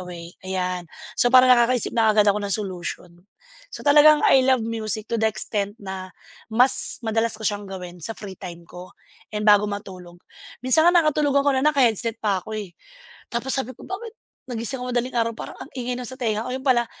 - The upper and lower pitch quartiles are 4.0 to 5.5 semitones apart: Yes, average, 4.6 semitones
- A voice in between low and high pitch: No, high, 220 Hz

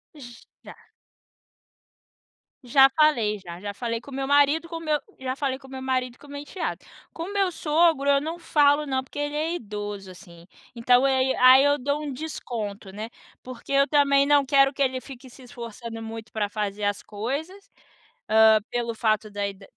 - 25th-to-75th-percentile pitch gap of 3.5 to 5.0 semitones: Yes, average, 4.6 semitones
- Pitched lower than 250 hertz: No, very high, 260 Hz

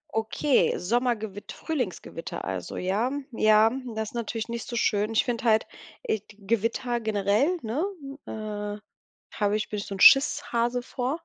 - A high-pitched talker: Yes, high, 220 Hz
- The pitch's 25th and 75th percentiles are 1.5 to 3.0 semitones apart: Yes, narrow, 2.6 semitones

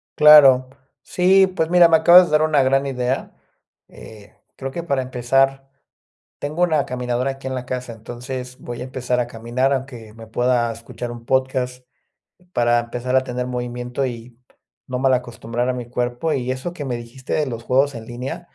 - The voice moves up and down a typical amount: No, narrow, 1.9 semitones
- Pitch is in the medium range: No, low, 125 Hz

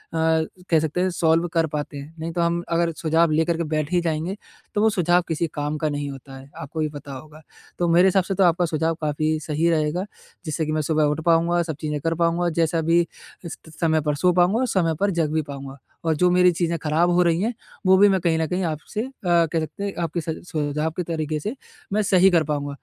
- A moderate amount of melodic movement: No, narrow, 2.2 semitones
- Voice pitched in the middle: Yes, medium, 165 Hz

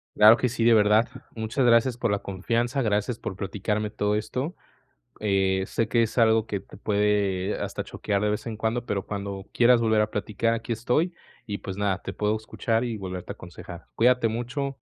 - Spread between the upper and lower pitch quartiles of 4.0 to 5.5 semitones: No, narrow, 2.4 semitones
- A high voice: No, low, 110 Hz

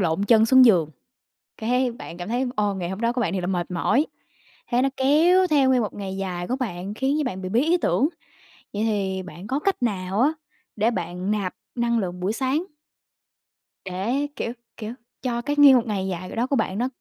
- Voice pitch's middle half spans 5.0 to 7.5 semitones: Yes, wide, 5.5 semitones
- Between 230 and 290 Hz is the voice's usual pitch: No, high, 220 Hz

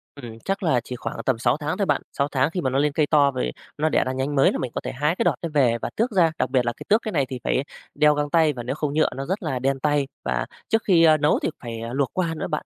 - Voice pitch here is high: No, medium, 145 Hz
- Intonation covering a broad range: No, average, 3.4 semitones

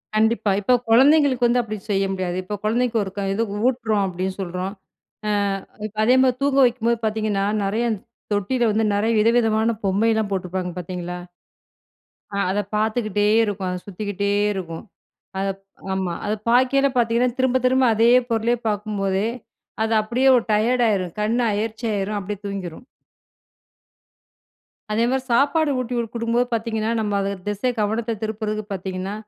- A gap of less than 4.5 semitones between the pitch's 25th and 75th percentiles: Yes, average, 3.2 semitones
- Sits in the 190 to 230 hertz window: Yes, high, 215 Hz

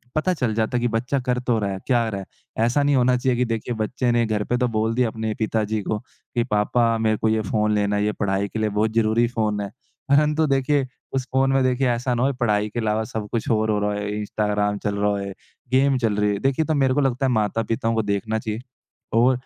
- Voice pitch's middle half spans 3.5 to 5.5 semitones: No, average, 3.1 semitones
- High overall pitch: No, low, 115 Hz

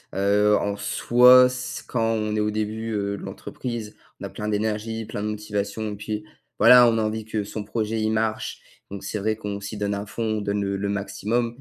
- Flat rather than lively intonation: Yes, narrow, 1.5 semitones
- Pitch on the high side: No, low, 105 Hz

